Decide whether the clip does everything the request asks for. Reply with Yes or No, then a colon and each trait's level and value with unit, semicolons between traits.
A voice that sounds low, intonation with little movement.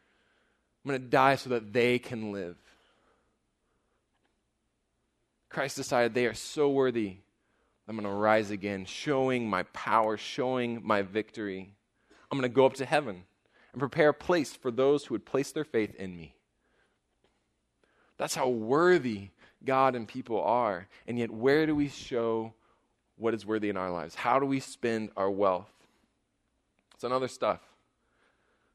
No: low, 115 Hz; average, 4.2 semitones